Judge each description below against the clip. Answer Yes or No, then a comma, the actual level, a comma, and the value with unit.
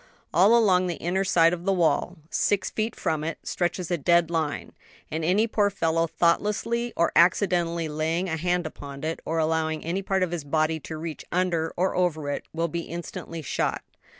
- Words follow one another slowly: No, average, 190 wpm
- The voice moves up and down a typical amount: No, narrow, 2.3 semitones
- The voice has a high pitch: No, medium, 170 Hz